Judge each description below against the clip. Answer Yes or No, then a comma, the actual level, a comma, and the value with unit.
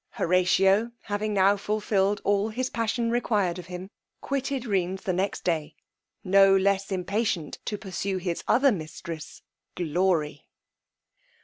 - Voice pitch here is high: Yes, high, 195 Hz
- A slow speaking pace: Yes, slow, 125 wpm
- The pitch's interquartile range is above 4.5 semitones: No, average, 2.9 semitones